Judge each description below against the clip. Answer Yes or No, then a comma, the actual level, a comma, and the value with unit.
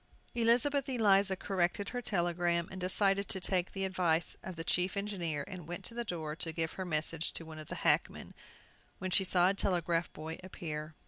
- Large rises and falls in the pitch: No, average, 2.9 semitones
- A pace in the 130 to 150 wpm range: No, average, 195 wpm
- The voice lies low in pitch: No, medium, 180 Hz